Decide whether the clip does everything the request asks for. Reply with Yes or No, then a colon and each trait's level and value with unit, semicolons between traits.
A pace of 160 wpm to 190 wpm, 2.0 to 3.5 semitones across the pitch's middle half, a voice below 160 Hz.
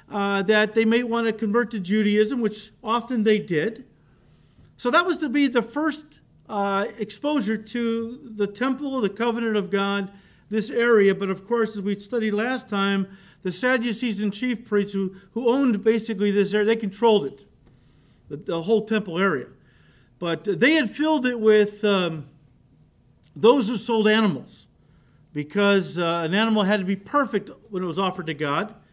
No: average, 170 wpm; average, 3.0 semitones; high, 215 Hz